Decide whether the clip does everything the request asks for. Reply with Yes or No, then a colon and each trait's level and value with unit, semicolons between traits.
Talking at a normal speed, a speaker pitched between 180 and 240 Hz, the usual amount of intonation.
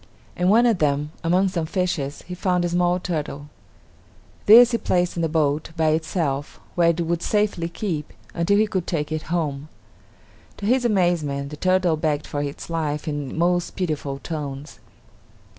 No: average, 170 wpm; medium, 165 Hz; average, 3.3 semitones